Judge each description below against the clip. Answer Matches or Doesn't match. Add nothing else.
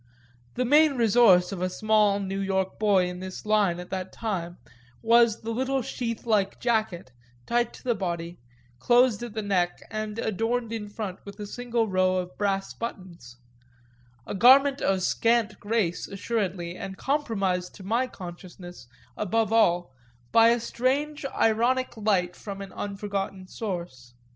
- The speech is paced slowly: Doesn't match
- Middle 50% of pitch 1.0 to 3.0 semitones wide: Doesn't match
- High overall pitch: Matches